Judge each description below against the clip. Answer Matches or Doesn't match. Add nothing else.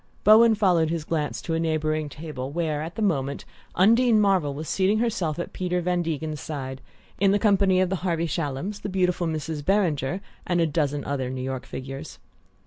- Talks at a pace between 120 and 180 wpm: Doesn't match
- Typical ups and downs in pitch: Matches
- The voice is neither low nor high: Matches